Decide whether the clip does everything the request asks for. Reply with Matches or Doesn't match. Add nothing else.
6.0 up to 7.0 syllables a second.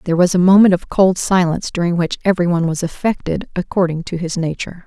Matches